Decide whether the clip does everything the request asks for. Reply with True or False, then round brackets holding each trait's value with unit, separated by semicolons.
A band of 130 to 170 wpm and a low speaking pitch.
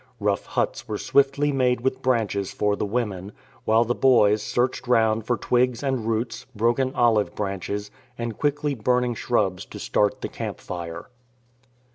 True (155 wpm; 115 Hz)